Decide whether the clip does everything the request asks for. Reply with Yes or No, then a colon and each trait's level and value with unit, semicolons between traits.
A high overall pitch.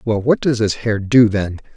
No: low, 110 Hz